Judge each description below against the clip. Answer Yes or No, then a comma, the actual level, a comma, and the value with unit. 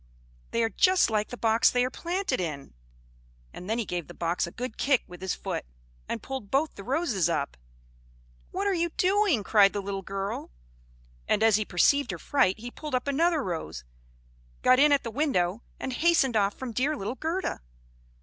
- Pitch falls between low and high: No, high, 240 Hz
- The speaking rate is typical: Yes, average, 195 wpm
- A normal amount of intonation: No, wide, 6.6 semitones